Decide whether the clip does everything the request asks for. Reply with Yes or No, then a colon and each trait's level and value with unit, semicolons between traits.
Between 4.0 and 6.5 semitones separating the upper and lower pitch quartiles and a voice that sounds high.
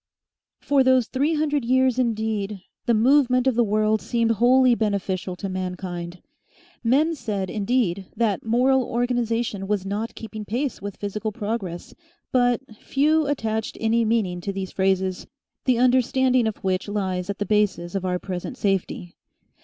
Yes: average, 4.4 semitones; high, 220 Hz